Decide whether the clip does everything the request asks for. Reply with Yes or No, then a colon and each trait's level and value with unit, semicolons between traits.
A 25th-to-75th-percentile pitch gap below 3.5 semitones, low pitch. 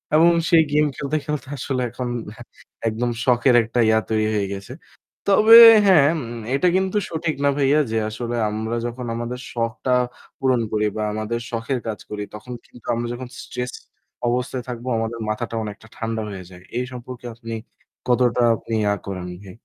Yes: average, 2.9 semitones; low, 120 Hz